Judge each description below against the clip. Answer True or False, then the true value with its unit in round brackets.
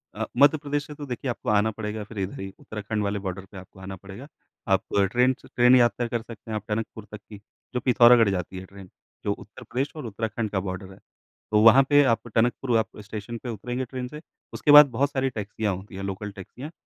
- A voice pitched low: True (110 Hz)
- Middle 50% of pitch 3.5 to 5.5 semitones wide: True (3.8 semitones)